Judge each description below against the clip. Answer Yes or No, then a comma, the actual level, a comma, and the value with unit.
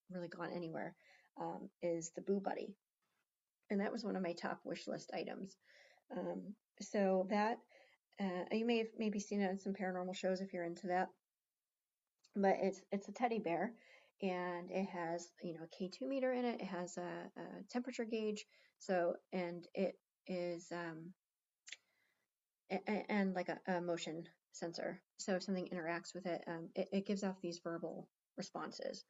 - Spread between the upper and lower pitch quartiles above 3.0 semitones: No, average, 2.7 semitones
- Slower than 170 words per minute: No, average, 175 wpm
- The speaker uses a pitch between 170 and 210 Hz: Yes, medium, 185 Hz